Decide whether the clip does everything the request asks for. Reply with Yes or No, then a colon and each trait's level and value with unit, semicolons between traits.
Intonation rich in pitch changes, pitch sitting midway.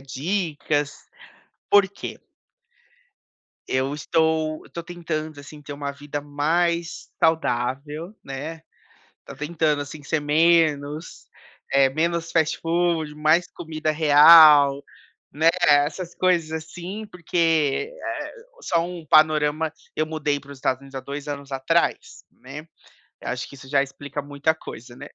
No: narrow, 2.5 semitones; medium, 155 Hz